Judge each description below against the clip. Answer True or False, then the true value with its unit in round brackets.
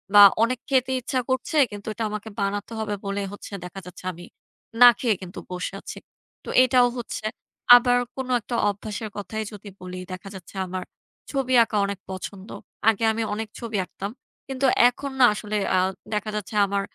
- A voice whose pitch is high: True (210 Hz)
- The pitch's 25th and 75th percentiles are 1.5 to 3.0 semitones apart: False (3.7 semitones)